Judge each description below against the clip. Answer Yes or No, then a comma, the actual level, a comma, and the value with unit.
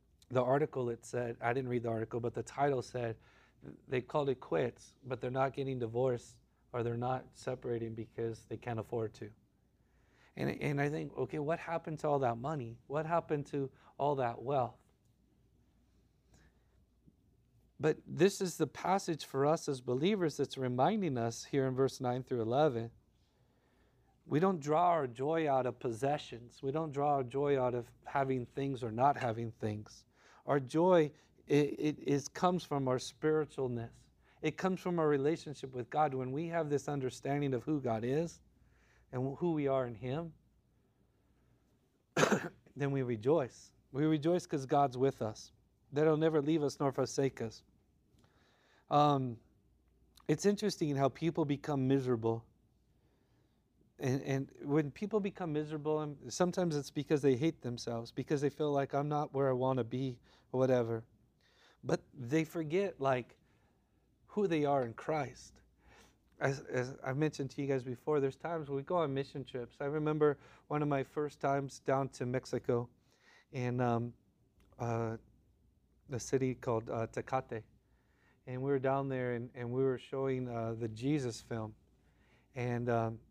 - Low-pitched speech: Yes, low, 130 Hz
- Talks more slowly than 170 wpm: Yes, average, 160 wpm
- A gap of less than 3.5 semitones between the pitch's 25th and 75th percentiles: No, average, 3.9 semitones